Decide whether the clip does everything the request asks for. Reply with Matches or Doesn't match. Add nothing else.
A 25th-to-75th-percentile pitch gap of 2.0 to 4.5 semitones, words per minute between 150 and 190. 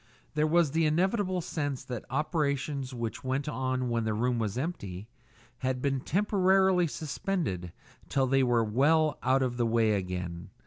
Doesn't match